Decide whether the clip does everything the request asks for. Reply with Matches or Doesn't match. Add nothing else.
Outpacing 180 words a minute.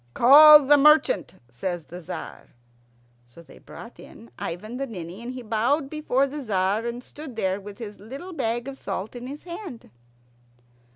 Doesn't match